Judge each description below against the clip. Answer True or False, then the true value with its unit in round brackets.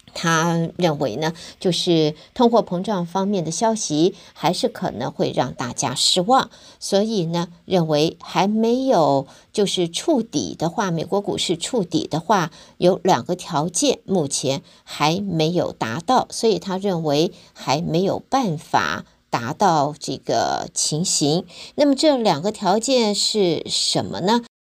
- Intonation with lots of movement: False (4.6 semitones)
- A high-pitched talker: False (180 Hz)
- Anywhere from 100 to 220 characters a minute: True (210 characters per minute)